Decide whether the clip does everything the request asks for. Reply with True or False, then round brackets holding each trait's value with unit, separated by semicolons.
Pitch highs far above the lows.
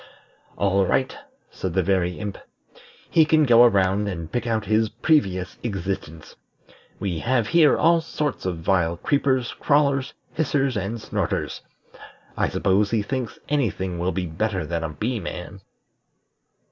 True (5.9 semitones)